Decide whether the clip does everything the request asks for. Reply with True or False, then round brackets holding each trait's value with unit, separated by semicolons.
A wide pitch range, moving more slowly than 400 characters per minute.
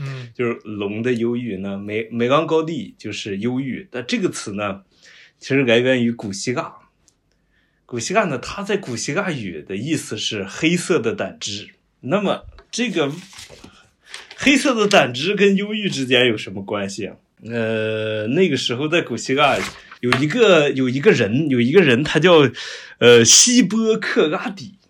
True (6.8 semitones; 235 characters per minute)